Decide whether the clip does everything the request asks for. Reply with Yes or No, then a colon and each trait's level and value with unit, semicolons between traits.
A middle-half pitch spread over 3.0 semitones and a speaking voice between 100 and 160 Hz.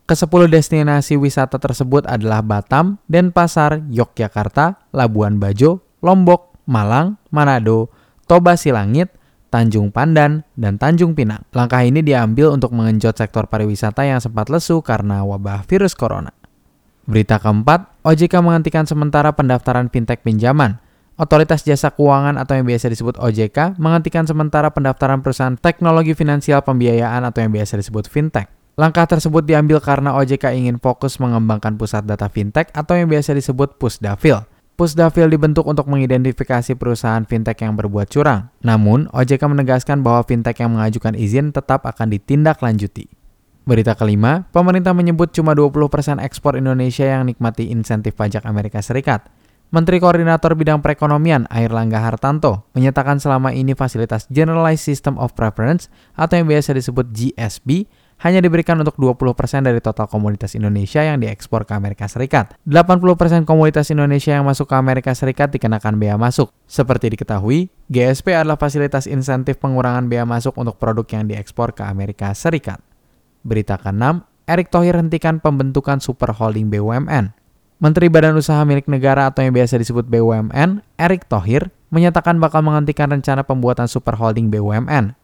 Yes: average, 5.2 semitones; low, 135 Hz